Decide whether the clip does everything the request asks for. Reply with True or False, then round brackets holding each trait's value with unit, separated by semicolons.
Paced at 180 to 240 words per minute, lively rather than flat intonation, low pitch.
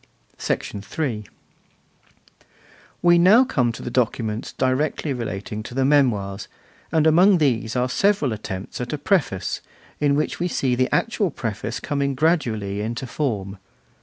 False (135 wpm; 5.9 semitones; 130 Hz)